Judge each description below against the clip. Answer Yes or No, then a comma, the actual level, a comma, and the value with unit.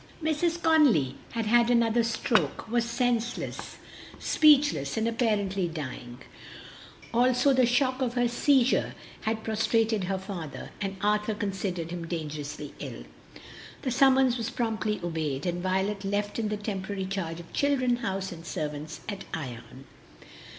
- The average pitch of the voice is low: No, high, 210 Hz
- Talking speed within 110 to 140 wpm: Yes, slow, 135 wpm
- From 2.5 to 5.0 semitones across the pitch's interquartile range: No, wide, 5.4 semitones